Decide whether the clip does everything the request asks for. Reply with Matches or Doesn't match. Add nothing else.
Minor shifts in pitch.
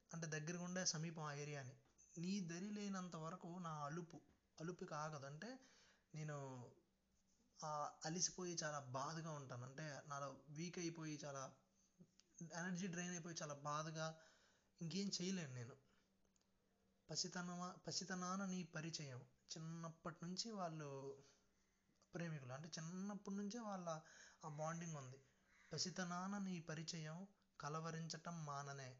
Doesn't match